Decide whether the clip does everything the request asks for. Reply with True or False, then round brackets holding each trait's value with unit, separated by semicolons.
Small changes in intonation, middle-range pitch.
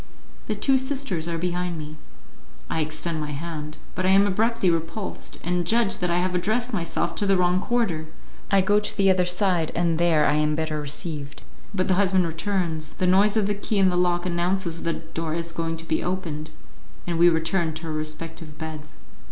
False (3.1 semitones; 175 Hz)